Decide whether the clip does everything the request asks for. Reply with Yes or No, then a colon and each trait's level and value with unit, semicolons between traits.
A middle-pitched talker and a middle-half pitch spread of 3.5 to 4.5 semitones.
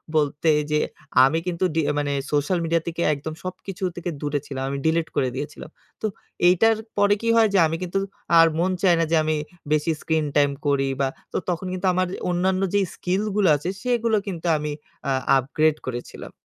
Yes: medium, 165 Hz; average, 4.0 semitones